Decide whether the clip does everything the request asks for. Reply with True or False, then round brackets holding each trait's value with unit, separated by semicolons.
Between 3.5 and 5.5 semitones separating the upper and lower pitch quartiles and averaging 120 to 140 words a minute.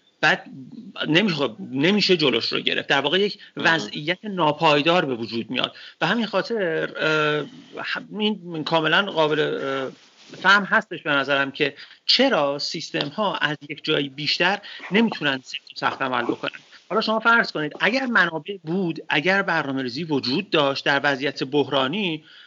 True (4.9 semitones; 135 wpm)